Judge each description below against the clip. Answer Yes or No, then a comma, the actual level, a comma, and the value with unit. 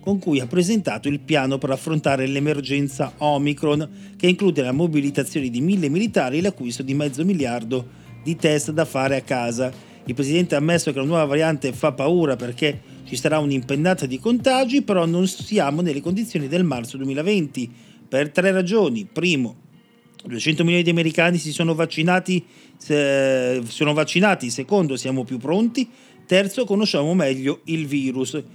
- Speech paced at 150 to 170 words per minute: Yes, average, 160 wpm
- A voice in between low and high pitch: Yes, medium, 150 Hz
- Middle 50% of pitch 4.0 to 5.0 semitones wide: Yes, average, 4.7 semitones